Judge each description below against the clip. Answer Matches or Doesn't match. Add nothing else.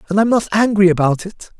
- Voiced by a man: Matches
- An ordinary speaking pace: Doesn't match